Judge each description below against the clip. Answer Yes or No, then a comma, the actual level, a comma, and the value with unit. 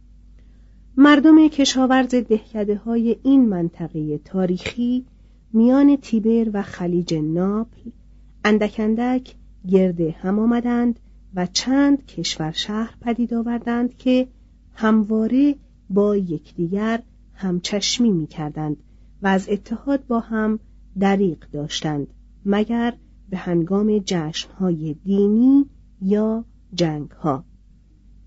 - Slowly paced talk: Yes, slow, 95 wpm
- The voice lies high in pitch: Yes, high, 210 Hz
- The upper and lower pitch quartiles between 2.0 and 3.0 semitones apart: No, average, 4.8 semitones